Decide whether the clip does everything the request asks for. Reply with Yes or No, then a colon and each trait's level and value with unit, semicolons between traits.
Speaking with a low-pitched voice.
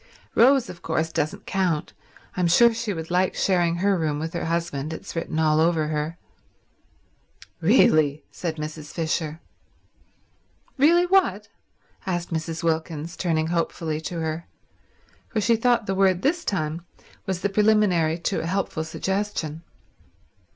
No: medium, 170 Hz